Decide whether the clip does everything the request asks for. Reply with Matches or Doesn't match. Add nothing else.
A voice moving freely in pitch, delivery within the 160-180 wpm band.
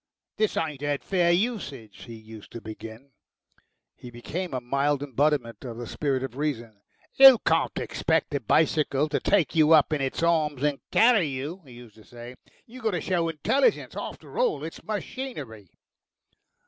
Matches